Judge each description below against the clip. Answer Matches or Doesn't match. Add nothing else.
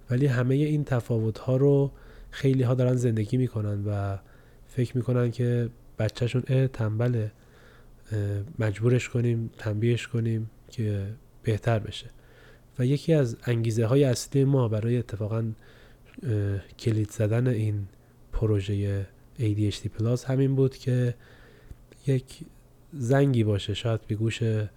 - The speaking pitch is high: Doesn't match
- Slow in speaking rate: Matches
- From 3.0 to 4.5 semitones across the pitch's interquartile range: Doesn't match